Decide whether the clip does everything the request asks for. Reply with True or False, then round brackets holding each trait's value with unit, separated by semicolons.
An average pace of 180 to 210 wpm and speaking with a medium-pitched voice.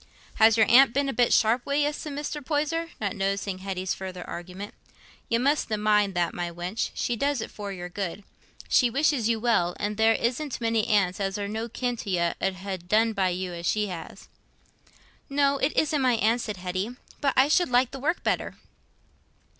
False (200 wpm; 220 Hz)